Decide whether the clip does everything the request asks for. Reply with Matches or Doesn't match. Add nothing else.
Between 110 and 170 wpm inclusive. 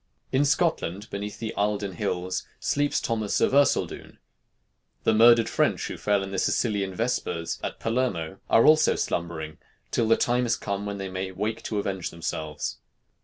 Matches